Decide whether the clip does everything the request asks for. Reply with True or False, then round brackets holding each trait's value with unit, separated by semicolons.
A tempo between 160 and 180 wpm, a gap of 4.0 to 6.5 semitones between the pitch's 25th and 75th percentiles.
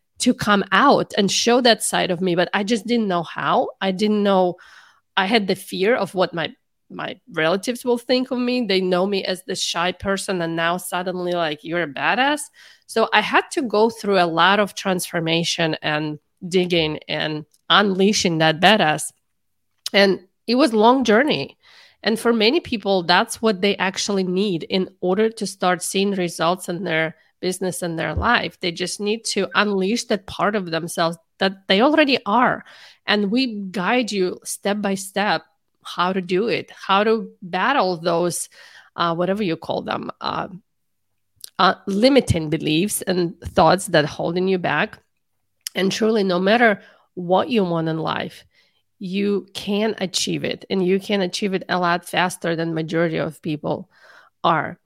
False (170 wpm; 3.2 semitones)